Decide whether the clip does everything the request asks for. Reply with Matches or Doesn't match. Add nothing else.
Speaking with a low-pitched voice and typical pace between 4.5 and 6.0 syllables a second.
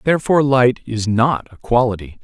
Matches